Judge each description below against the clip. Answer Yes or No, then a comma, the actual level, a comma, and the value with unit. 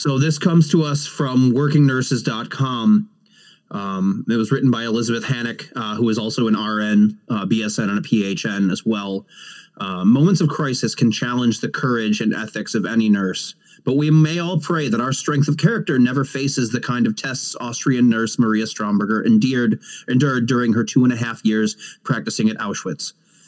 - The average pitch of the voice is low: Yes, low, 125 Hz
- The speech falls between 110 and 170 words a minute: No, average, 185 wpm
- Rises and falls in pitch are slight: No, average, 4.6 semitones